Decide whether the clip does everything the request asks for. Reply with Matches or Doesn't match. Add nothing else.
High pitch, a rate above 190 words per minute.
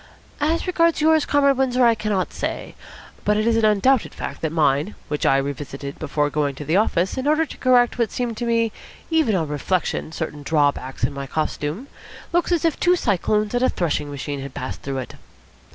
Matches